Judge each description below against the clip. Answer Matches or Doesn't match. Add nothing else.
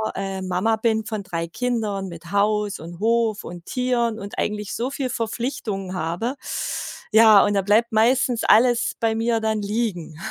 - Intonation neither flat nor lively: Matches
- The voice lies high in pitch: Matches